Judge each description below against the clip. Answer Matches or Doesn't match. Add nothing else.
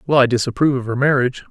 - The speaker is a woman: Doesn't match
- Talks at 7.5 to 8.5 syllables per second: Matches